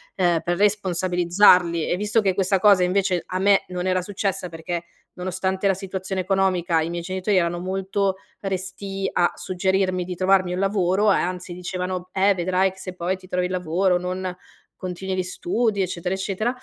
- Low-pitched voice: No, medium, 185 Hz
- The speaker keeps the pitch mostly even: Yes, narrow, 1.3 semitones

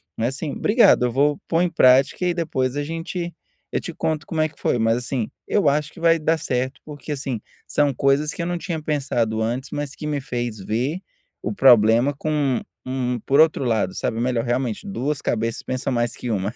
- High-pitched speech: No, low, 135 Hz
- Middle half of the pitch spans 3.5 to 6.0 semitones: Yes, average, 4.1 semitones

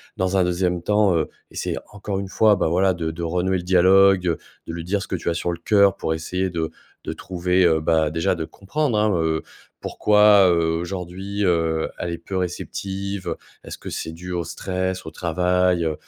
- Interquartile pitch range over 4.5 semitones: No, narrow, 2.4 semitones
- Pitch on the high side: No, very low, 90 Hz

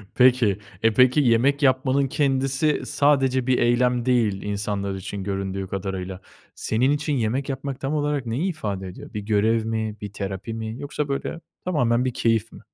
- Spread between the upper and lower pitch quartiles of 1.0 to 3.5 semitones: No, average, 4.7 semitones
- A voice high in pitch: No, low, 120 Hz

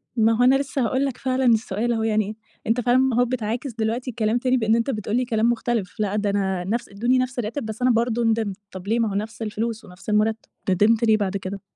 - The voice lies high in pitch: Yes, high, 225 Hz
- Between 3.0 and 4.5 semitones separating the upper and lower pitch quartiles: No, narrow, 2.5 semitones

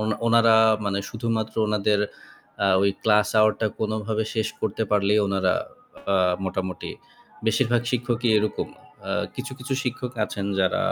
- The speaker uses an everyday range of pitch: No, narrow, 2.3 semitones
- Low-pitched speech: Yes, low, 110 Hz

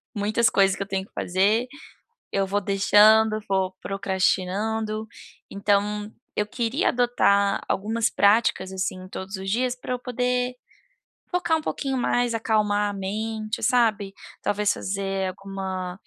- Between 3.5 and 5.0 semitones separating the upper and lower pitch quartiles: No, average, 2.8 semitones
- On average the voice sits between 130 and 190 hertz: No, high, 205 Hz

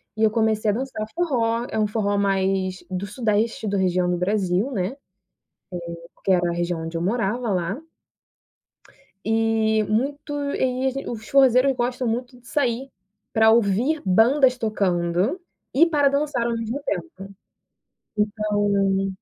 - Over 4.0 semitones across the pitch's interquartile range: Yes, average, 4.4 semitones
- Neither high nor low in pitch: No, high, 220 Hz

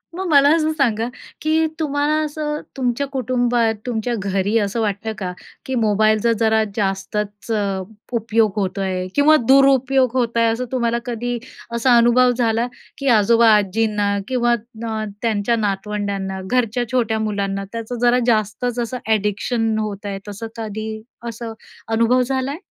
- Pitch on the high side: Yes, high, 230 Hz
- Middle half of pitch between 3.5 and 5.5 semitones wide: No, average, 3.0 semitones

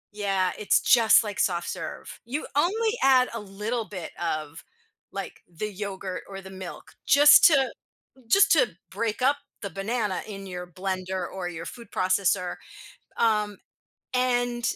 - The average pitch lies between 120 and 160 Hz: No, high, 205 Hz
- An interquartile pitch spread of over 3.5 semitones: Yes, average, 4.6 semitones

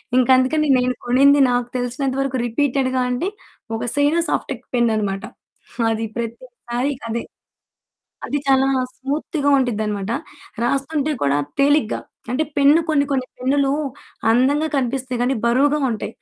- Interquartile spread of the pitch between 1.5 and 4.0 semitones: Yes, average, 2.9 semitones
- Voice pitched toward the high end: Yes, very high, 260 Hz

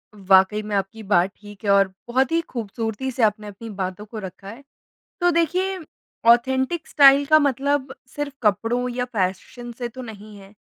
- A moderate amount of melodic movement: Yes, average, 4.8 semitones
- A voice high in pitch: Yes, high, 225 Hz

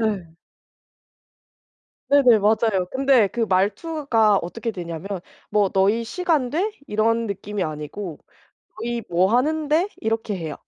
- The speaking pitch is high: Yes, high, 220 Hz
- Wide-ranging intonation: No, average, 4.5 semitones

